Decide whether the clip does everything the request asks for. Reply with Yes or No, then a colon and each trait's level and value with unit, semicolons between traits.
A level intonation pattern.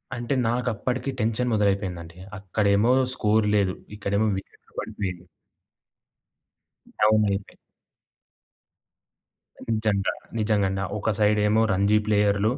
Yes: narrow, 1.8 semitones